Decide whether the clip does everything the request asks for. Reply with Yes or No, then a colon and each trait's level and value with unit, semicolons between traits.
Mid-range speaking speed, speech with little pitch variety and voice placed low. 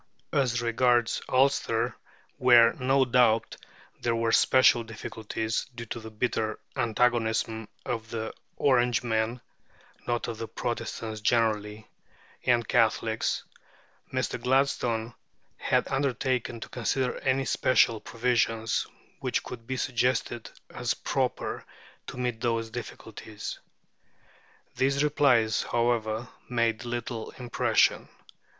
No: slow, 105 wpm; narrow, 2.0 semitones; low, 120 Hz